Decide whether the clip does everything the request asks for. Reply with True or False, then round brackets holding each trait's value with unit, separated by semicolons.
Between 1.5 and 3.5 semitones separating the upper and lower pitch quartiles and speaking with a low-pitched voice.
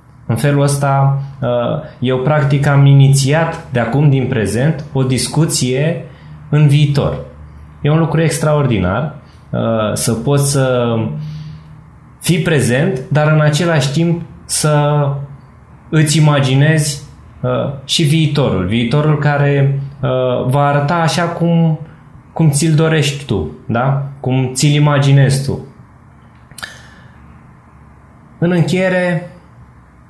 False (3.0 semitones; 145 Hz)